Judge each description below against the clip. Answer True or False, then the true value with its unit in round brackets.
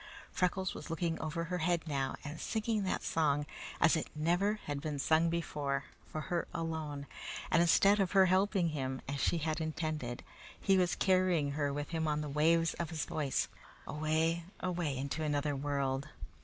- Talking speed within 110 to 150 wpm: False (175 wpm)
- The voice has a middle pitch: True (160 Hz)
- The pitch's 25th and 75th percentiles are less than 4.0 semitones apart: True (2.9 semitones)